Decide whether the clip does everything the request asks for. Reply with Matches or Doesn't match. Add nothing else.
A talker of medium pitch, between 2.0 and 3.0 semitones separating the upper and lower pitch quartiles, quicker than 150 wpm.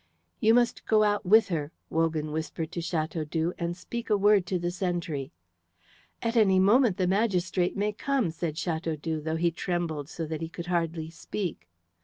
Doesn't match